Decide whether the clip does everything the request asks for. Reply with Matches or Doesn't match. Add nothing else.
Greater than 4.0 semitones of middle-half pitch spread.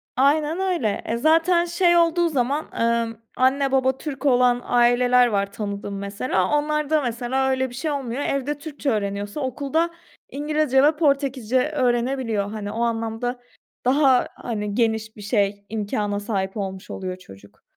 Matches